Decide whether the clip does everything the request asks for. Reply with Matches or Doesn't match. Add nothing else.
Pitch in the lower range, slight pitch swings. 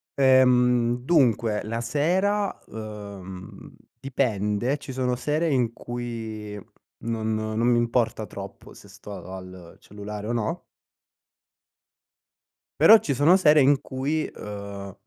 Doesn't match